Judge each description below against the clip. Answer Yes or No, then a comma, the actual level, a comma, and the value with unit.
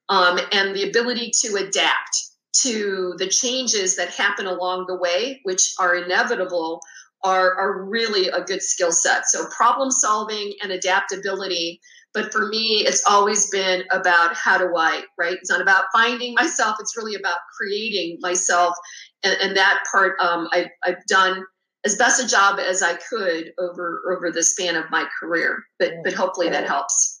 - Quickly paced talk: No, average, 170 wpm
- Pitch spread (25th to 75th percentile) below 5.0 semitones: Yes, average, 2.9 semitones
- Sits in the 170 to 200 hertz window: Yes, high, 190 Hz